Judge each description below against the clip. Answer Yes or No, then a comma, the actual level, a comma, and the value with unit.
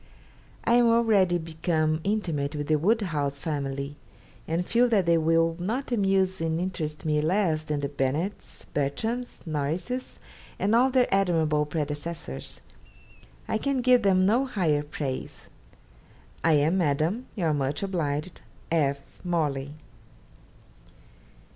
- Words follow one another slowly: Yes, slow, 125 wpm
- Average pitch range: Yes, average, 5.0 semitones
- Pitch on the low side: No, medium, 165 Hz